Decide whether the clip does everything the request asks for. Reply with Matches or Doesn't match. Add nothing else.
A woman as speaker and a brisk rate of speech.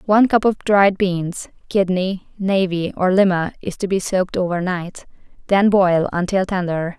Doesn't match